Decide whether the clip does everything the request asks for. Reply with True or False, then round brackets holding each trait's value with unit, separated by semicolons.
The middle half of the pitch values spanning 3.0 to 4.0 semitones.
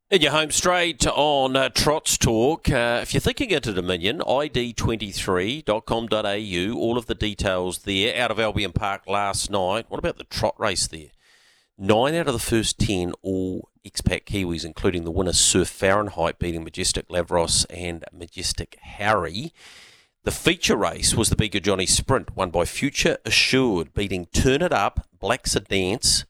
False (4.7 semitones)